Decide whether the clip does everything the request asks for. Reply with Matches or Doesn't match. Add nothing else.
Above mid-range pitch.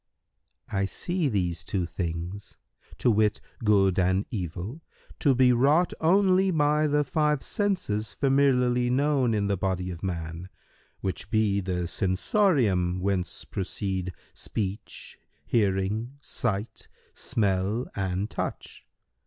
Doesn't match